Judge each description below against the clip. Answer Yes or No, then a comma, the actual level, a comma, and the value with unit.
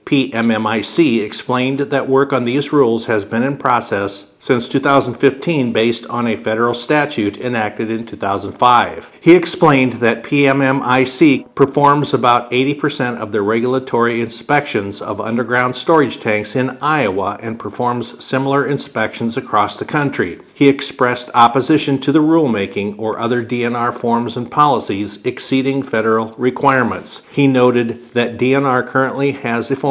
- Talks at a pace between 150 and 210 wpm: No, slow, 135 wpm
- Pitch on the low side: Yes, low, 125 Hz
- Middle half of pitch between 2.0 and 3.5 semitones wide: Yes, average, 3.1 semitones